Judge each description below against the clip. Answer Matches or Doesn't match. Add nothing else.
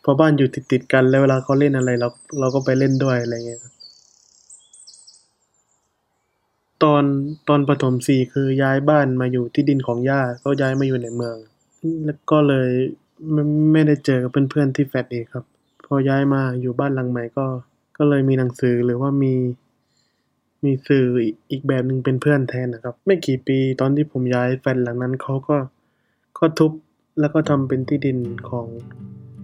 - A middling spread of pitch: Doesn't match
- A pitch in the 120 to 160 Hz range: Matches